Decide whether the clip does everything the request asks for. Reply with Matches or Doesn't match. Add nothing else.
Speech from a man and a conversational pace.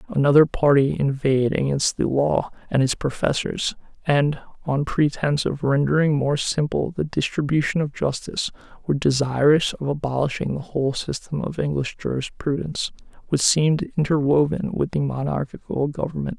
Doesn't match